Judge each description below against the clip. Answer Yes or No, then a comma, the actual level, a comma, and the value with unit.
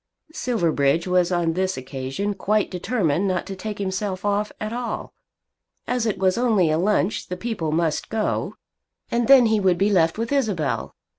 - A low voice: No, high, 195 Hz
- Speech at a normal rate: Yes, average, 170 wpm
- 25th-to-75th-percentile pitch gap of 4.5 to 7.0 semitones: No, average, 4.1 semitones